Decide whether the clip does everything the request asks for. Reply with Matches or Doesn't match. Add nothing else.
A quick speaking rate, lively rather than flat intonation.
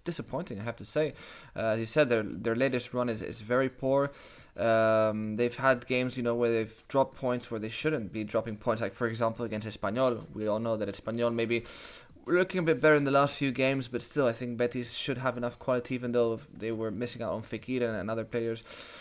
Doesn't match